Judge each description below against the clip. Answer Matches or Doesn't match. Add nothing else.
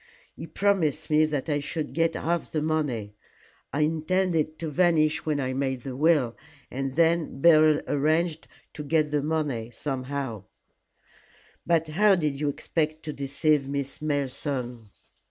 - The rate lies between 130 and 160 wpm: Matches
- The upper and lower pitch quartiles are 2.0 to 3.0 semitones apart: Matches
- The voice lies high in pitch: Doesn't match